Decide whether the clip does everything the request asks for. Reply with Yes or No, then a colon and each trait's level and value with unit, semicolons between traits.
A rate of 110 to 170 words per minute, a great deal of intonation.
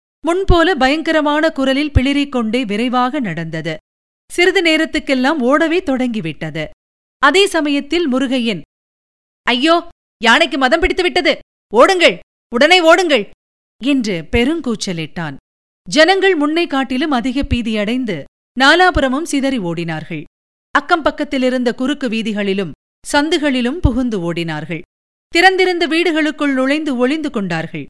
No: average, 95 wpm; wide, 6.0 semitones